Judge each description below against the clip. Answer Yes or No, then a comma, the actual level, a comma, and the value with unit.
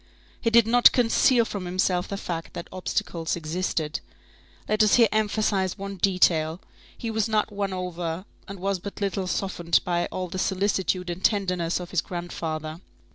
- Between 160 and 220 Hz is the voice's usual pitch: Yes, medium, 185 Hz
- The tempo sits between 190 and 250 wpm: No, average, 165 wpm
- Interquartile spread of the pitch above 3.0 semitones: No, average, 2.7 semitones